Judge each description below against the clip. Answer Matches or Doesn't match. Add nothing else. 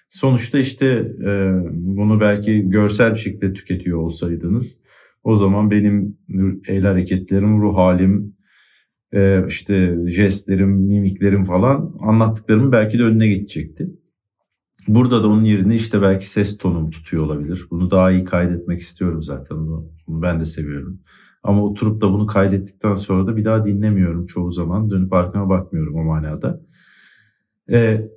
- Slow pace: Doesn't match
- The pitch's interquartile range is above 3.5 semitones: Doesn't match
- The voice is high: Doesn't match